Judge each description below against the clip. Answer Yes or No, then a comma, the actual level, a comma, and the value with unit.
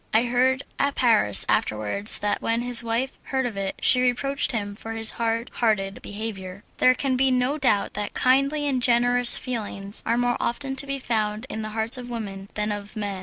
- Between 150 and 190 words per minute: No, average, 200 wpm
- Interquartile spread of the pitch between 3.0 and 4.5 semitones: Yes, average, 3.3 semitones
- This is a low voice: No, high, 230 Hz